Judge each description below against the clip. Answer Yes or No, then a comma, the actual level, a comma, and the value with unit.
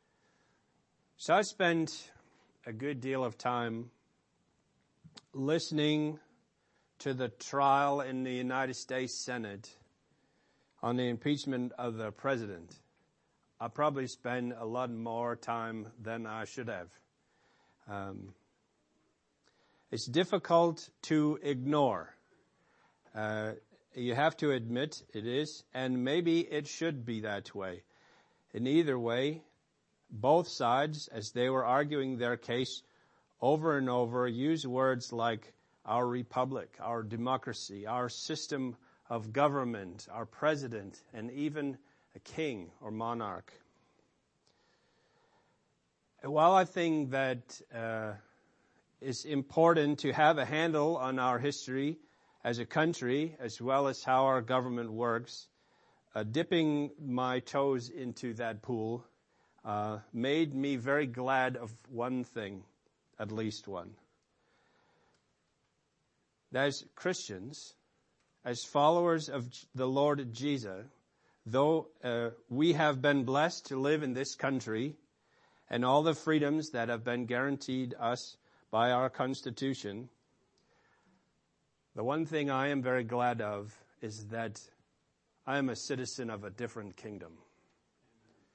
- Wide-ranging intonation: No, average, 3.6 semitones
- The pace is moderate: No, slow, 120 wpm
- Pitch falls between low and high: No, low, 130 Hz